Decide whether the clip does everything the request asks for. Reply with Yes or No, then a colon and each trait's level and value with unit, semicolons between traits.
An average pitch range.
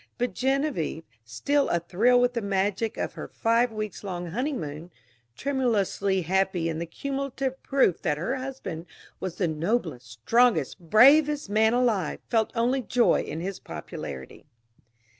No: wide, 6.7 semitones